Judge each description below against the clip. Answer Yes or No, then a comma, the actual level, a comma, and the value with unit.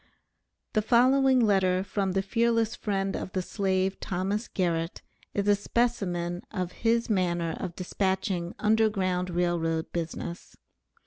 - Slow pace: Yes, slow, 130 wpm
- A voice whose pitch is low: No, high, 190 Hz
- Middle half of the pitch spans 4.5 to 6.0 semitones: No, average, 3.4 semitones